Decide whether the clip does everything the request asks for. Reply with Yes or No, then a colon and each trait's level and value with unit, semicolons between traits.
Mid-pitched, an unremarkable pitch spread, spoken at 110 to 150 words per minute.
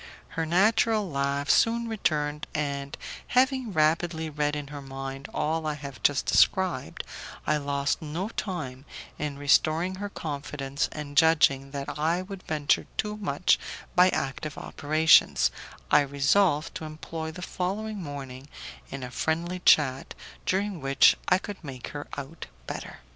Yes: medium, 155 Hz; average, 4.3 semitones; average, 140 wpm